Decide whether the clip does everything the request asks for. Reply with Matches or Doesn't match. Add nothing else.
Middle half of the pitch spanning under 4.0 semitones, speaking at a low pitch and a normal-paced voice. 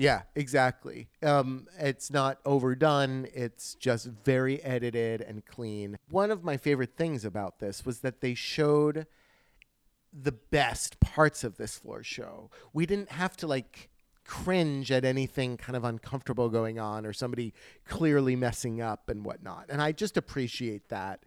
Matches